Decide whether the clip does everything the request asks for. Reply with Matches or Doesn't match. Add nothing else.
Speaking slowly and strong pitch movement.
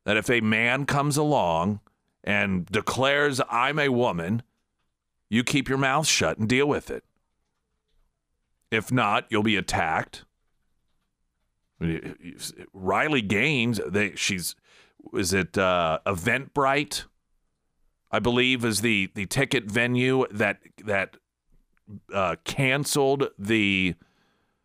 Matches